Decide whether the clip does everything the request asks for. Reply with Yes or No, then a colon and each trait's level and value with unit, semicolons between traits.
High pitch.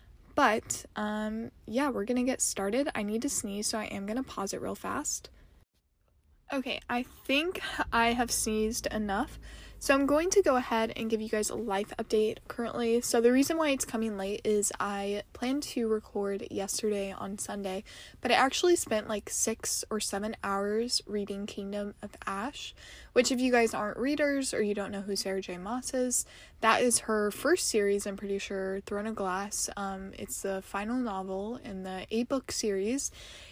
Yes: high, 220 Hz